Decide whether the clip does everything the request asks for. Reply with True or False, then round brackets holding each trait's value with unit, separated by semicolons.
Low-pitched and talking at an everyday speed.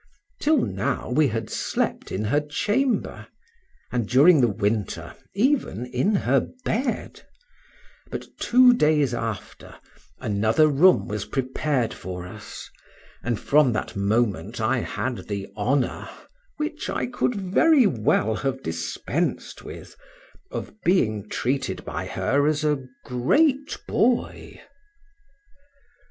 False (130 Hz; 115 wpm)